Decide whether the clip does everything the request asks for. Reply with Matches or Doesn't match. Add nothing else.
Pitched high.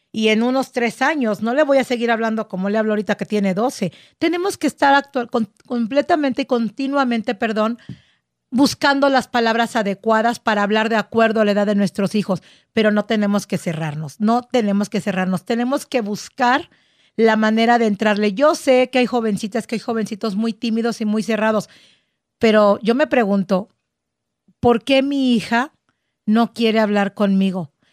Matches